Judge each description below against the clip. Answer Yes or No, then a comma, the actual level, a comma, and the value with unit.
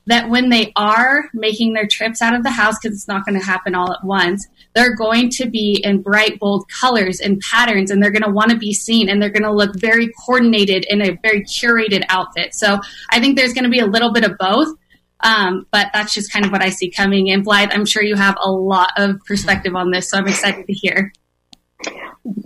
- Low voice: No, high, 205 Hz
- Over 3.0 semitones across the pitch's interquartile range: No, narrow, 2.4 semitones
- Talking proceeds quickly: Yes, fast, 240 wpm